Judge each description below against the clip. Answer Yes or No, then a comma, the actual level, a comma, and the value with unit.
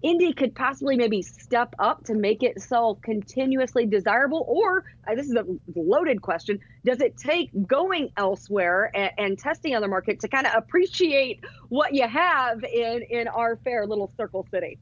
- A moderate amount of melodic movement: Yes, average, 4.7 semitones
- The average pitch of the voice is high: Yes, high, 235 Hz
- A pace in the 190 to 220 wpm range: No, average, 175 wpm